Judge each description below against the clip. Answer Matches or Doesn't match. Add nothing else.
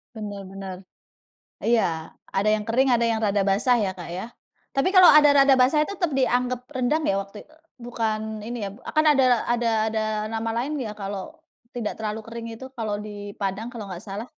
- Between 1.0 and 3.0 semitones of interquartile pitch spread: Doesn't match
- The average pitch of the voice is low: Doesn't match